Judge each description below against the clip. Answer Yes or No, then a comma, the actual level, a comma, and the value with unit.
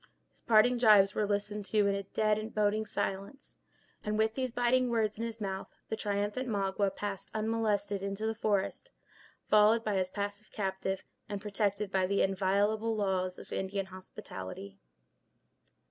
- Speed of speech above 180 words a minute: No, average, 155 wpm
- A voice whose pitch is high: Yes, high, 205 Hz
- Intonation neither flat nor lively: No, narrow, 1.9 semitones